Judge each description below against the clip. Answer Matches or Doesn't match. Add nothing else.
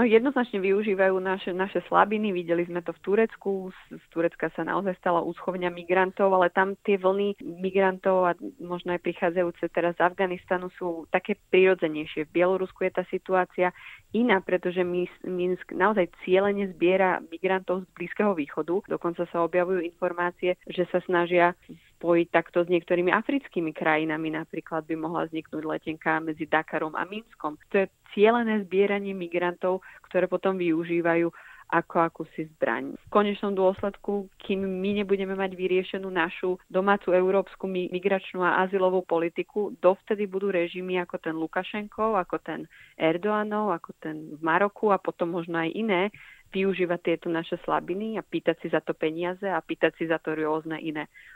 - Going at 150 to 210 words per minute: Matches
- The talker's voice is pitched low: Doesn't match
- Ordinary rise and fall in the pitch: Doesn't match